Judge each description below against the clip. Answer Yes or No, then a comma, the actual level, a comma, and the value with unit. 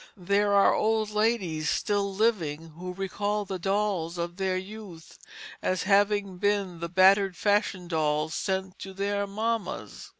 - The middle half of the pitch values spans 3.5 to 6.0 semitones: No, narrow, 2.5 semitones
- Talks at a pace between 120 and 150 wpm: Yes, average, 140 wpm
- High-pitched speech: Yes, high, 195 Hz